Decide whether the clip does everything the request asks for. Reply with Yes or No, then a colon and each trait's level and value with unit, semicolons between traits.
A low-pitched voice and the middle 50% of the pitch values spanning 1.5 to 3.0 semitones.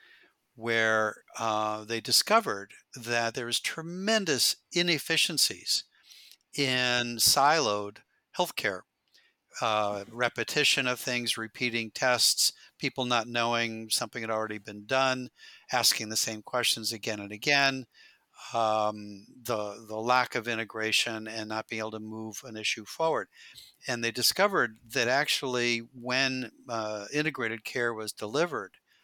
Yes: low, 115 Hz; narrow, 2.5 semitones